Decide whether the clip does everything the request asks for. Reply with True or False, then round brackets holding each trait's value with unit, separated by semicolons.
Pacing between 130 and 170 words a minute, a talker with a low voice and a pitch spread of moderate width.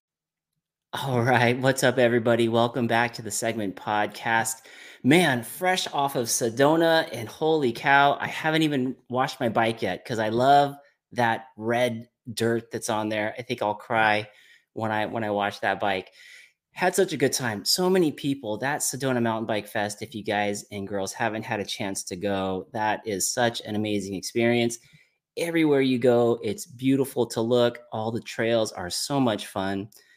False (180 wpm; 120 Hz; 3.9 semitones)